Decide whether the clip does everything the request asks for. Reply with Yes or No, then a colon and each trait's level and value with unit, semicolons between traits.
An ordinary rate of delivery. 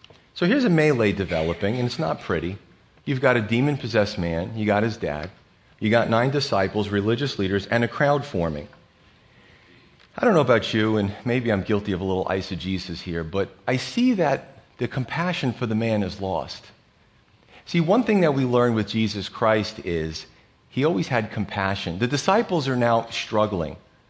Yes: average, 180 wpm